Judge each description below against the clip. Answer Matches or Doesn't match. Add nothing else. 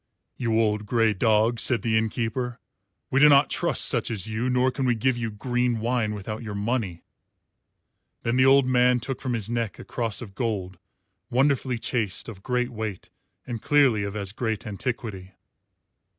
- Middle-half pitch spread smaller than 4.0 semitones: Matches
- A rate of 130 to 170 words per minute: Doesn't match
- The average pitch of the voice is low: Matches